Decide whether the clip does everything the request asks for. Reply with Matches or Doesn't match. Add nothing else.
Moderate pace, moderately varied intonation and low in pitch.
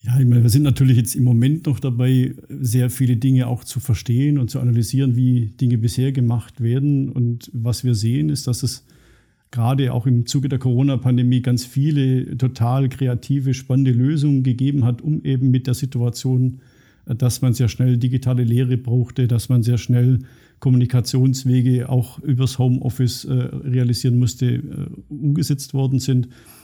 Doesn't match